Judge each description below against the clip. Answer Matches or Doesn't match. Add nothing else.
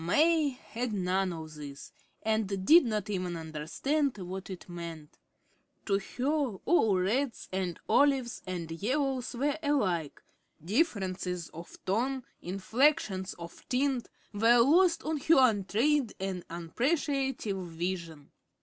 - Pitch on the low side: Doesn't match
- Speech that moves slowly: Matches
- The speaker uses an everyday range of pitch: Doesn't match